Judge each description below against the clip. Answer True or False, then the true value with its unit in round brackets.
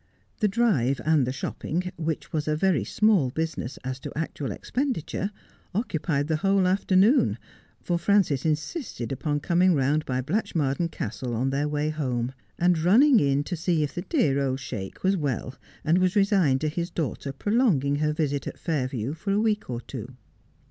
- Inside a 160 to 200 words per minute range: True (175 wpm)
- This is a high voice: False (155 Hz)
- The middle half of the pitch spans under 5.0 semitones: False (5.3 semitones)